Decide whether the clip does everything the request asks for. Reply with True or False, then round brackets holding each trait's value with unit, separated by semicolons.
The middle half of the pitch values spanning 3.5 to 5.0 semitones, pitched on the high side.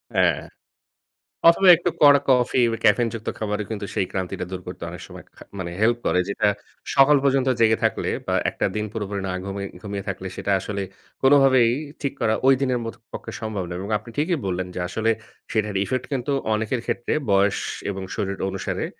False (4.6 semitones; 110 Hz)